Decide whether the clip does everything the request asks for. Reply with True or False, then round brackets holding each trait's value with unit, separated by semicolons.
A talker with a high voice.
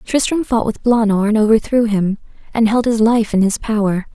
True (220 Hz)